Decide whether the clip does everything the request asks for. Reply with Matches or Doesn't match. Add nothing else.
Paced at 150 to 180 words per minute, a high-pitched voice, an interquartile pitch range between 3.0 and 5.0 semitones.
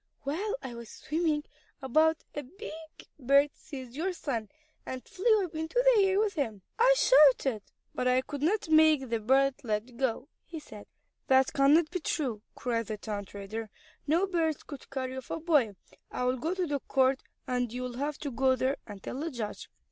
Doesn't match